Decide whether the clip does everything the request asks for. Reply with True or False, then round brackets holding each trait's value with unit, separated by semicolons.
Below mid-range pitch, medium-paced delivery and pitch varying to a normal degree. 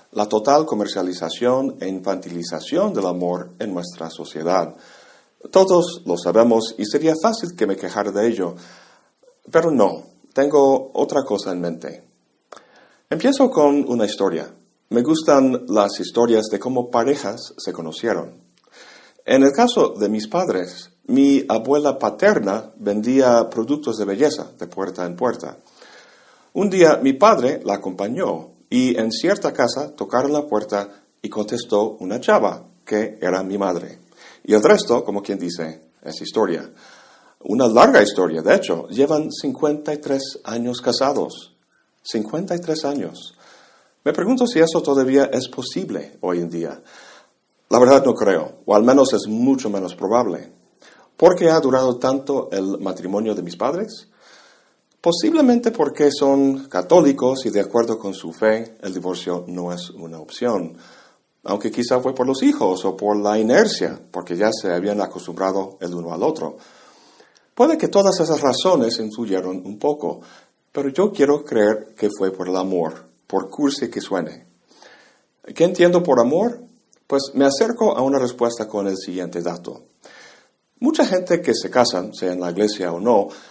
False (115 Hz; 150 wpm; 7.0 semitones)